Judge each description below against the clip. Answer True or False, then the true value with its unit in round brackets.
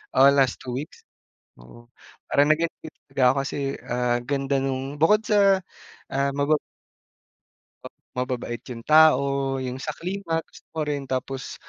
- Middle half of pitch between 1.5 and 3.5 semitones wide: True (3.1 semitones)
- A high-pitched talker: False (140 Hz)